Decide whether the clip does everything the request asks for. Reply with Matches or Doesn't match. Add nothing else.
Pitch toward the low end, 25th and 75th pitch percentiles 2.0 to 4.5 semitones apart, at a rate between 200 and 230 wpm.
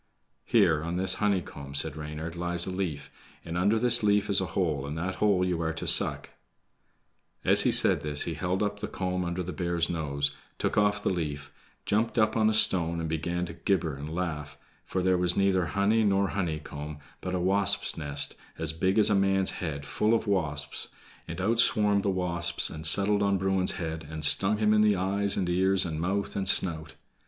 Matches